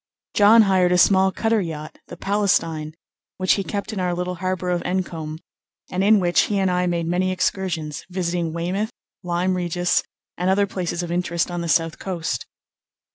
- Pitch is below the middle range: No, medium, 180 Hz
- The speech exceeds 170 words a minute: Yes, average, 180 wpm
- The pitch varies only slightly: Yes, narrow, 1.9 semitones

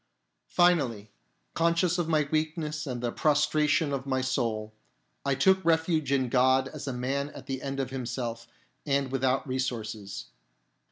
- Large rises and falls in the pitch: No, average, 3.4 semitones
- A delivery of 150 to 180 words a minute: Yes, average, 155 wpm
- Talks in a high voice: No, low, 135 Hz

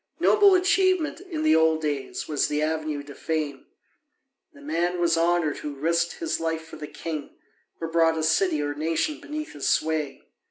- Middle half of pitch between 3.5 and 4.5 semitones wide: Yes, average, 4.1 semitones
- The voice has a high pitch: No, medium, 160 Hz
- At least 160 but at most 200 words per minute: Yes, average, 175 wpm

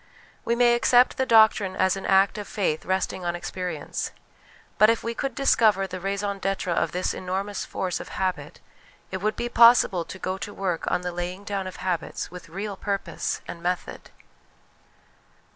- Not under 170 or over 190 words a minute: Yes, average, 175 wpm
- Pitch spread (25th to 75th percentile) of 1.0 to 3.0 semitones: Yes, average, 2.7 semitones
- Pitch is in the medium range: No, high, 195 Hz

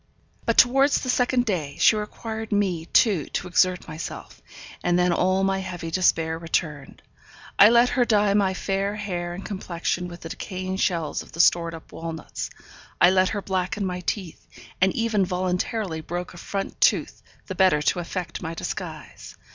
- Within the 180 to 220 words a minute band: No, average, 170 wpm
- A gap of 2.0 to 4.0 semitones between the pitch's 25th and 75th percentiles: Yes, average, 3.0 semitones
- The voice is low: No, medium, 185 Hz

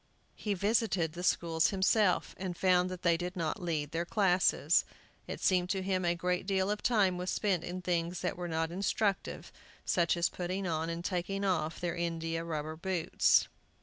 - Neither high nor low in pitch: Yes, medium, 180 Hz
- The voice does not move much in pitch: Yes, narrow, 2.1 semitones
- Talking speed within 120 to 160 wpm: No, average, 180 wpm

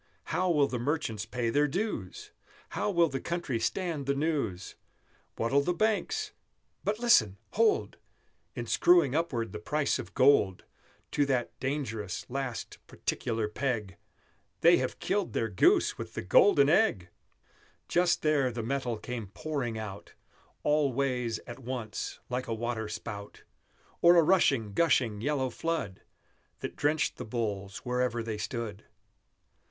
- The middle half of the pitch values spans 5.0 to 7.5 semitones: Yes, wide, 5.5 semitones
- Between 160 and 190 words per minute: No, average, 140 wpm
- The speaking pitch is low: Yes, low, 130 Hz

